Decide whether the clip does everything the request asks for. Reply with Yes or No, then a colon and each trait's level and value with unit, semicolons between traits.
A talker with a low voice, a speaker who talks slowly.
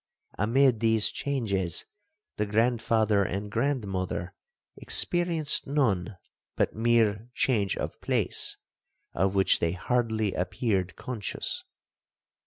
Yes: low, 110 Hz; slow, 95 wpm